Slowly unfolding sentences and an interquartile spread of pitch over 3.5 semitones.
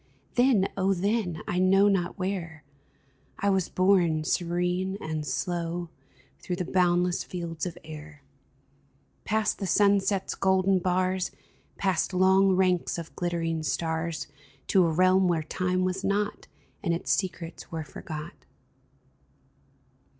No: slow, 130 wpm; narrow, 2.5 semitones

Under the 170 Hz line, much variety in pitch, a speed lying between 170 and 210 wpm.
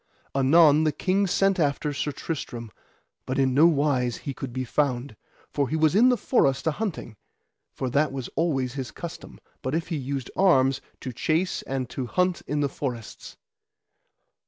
No: medium, 140 Hz; average, 4.0 semitones; average, 175 wpm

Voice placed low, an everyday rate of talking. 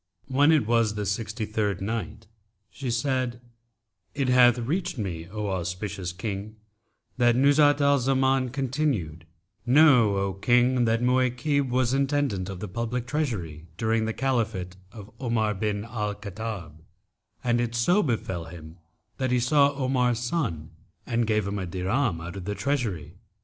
Yes: low, 115 Hz; average, 150 wpm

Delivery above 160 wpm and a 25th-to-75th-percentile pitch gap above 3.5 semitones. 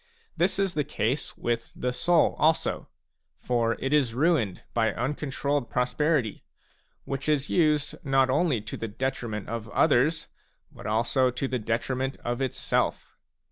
No: average, 140 wpm; average, 4.2 semitones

